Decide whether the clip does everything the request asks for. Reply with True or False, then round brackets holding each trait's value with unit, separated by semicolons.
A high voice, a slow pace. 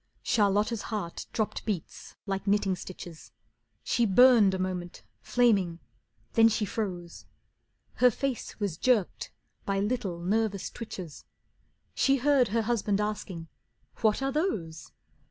True (210 Hz; 120 wpm)